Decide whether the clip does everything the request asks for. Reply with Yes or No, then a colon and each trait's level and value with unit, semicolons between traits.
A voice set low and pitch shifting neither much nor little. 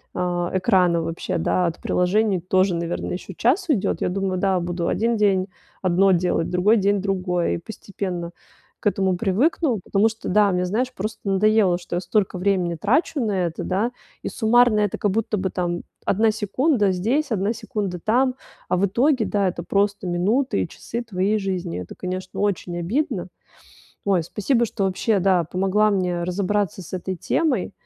No: high, 195 Hz; average, 3.2 semitones